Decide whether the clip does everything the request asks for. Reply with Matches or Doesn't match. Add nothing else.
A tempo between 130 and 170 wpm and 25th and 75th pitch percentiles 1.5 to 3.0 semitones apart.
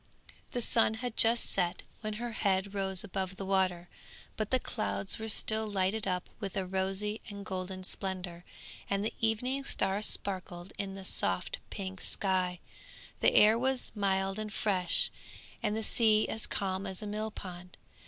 Matches